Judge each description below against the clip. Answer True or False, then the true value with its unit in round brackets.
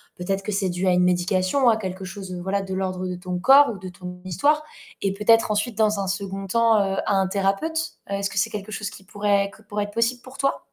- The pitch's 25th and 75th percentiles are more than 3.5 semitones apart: False (2.6 semitones)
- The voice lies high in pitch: True (195 Hz)